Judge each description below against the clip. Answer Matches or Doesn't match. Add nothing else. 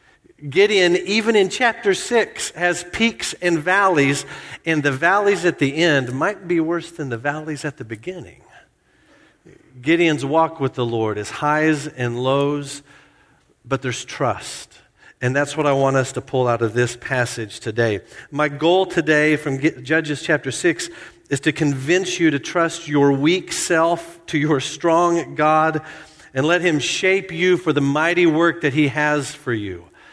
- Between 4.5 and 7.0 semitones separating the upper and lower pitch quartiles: Doesn't match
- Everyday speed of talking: Matches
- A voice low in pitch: Doesn't match